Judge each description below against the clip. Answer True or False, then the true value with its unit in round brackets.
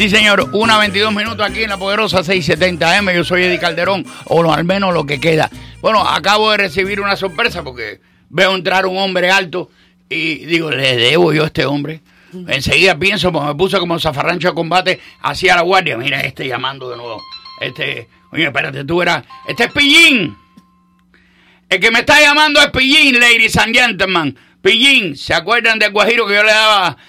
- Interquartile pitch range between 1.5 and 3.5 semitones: False (4.3 semitones)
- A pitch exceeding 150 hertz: True (190 Hz)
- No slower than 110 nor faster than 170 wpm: False (185 wpm)